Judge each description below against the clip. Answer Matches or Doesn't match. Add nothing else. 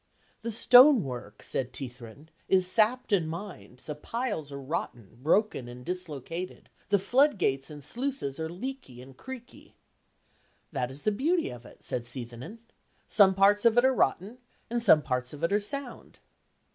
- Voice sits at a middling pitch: Matches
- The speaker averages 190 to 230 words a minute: Doesn't match